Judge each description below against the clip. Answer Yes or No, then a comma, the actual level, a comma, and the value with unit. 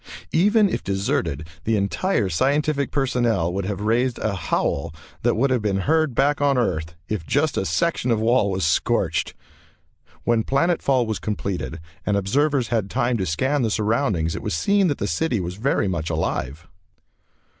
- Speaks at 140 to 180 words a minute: Yes, average, 175 wpm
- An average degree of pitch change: No, wide, 6.6 semitones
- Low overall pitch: Yes, low, 110 Hz